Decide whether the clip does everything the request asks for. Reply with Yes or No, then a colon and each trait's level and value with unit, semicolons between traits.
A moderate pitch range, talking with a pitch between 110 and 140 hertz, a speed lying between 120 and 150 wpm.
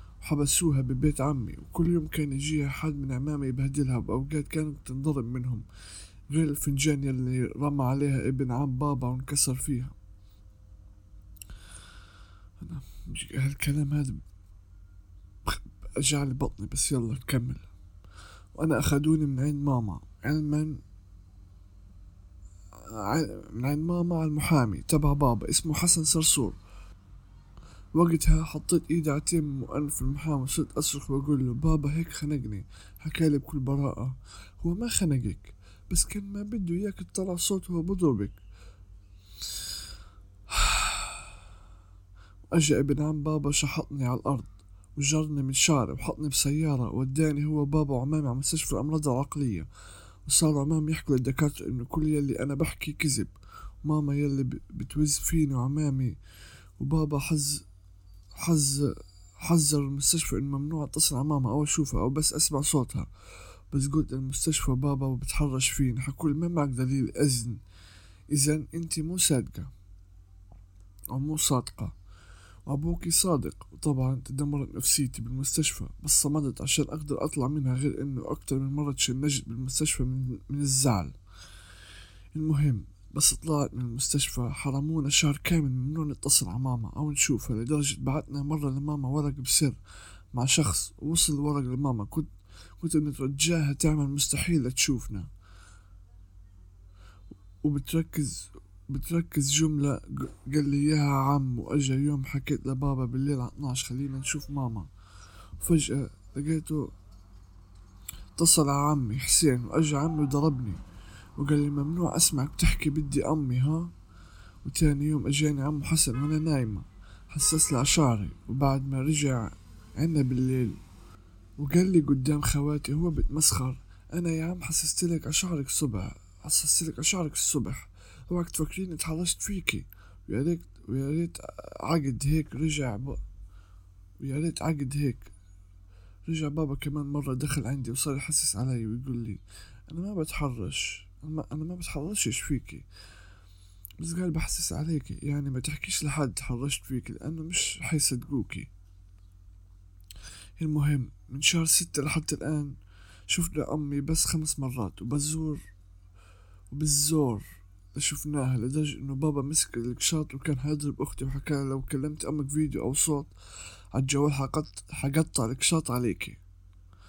No: wide, 7.8 semitones; low, 135 Hz; average, 125 wpm